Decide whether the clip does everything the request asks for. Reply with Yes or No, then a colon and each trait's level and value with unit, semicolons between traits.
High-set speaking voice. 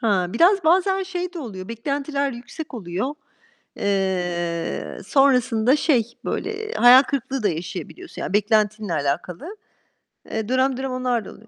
Yes: high, 245 Hz